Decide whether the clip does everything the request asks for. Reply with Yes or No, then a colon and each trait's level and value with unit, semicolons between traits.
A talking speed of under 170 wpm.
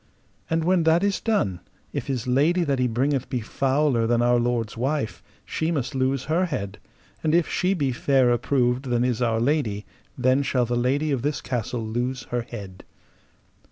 No: average, 185 wpm